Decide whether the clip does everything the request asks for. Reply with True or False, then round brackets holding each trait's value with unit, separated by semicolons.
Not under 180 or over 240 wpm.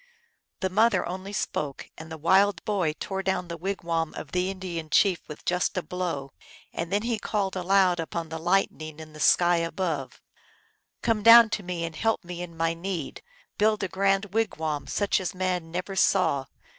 True (190 wpm)